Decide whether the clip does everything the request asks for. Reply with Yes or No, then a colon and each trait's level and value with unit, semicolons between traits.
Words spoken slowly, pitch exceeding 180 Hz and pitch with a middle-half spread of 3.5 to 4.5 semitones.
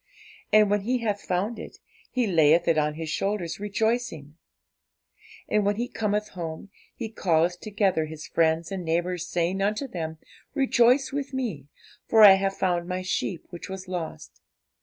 No: average, 160 wpm; high, 190 Hz; average, 4.2 semitones